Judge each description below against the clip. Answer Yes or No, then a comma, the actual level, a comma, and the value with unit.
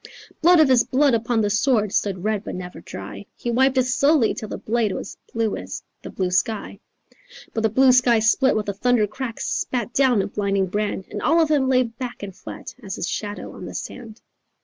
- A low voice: No, high, 230 Hz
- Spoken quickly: Yes, fast, 215 wpm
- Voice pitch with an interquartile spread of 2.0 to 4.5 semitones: Yes, average, 3.8 semitones